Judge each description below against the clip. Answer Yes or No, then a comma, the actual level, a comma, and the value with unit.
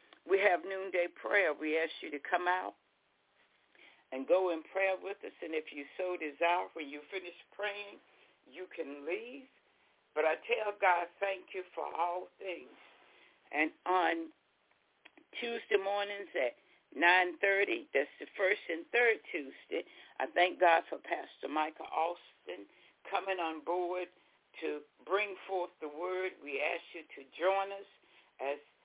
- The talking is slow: No, average, 150 wpm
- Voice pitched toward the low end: No, medium, 180 Hz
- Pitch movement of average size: Yes, average, 3.0 semitones